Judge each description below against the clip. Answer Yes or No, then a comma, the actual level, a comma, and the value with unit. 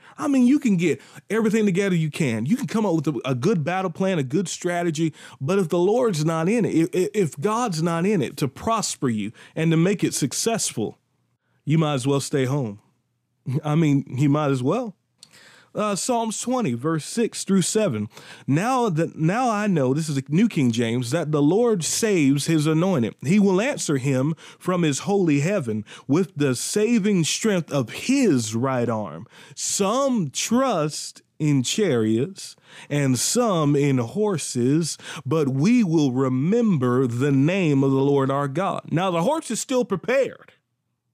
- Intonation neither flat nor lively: No, wide, 6.8 semitones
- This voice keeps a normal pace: Yes, average, 175 wpm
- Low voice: No, medium, 165 Hz